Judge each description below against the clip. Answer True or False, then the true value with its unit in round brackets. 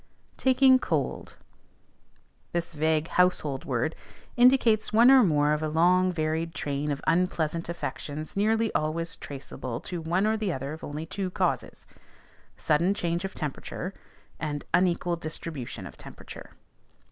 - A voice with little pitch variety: False (3.6 semitones)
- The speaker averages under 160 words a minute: True (135 wpm)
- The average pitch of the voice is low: False (165 Hz)